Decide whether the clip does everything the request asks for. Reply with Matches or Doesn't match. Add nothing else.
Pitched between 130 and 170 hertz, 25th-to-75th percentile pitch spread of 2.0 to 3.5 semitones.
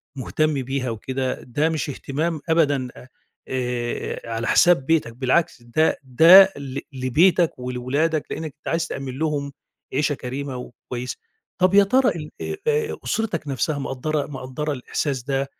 Doesn't match